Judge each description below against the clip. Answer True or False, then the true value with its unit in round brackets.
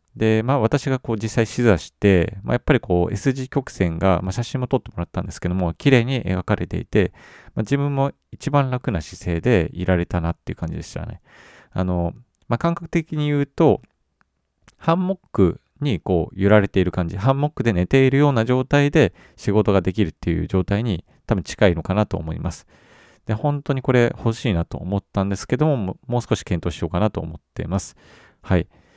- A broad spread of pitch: True (6.5 semitones)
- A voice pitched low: True (110 Hz)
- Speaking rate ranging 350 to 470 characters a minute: True (390 characters per minute)